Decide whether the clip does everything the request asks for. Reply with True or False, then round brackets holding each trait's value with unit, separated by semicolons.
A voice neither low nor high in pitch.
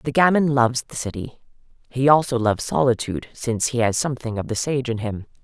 False (125 Hz)